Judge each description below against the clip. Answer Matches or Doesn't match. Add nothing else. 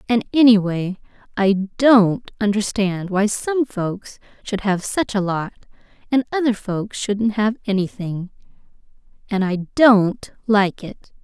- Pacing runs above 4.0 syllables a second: Doesn't match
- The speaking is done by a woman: Matches